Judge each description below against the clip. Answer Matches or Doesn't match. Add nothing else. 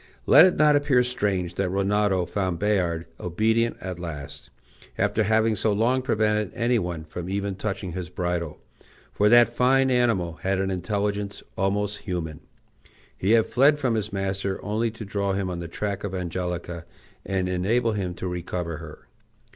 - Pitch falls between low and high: Doesn't match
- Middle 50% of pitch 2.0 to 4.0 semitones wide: Matches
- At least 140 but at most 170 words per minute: Matches